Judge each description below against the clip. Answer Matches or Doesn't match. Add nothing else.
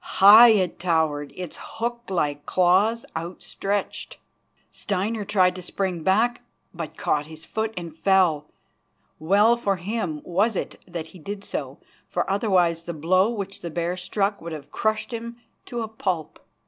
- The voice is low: Doesn't match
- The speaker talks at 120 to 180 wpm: Matches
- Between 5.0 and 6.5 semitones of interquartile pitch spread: Doesn't match